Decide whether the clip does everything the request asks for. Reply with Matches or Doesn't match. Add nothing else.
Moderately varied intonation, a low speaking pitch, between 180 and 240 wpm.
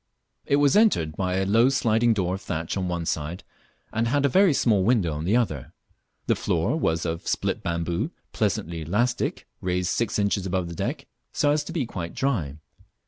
Doesn't match